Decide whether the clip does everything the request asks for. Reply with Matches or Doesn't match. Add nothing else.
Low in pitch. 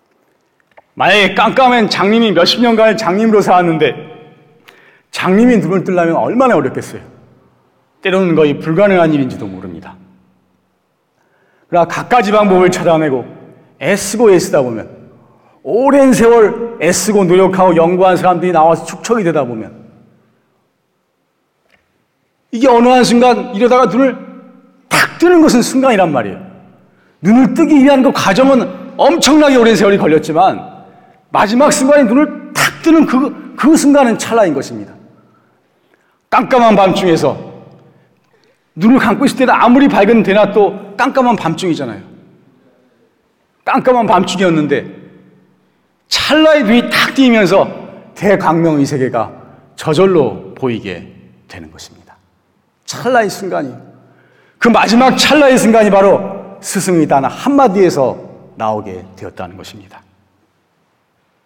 Doesn't match